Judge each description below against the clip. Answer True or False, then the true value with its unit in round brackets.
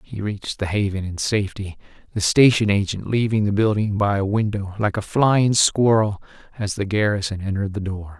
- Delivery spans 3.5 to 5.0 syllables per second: False (5.3 syllables/s)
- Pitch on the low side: True (100 Hz)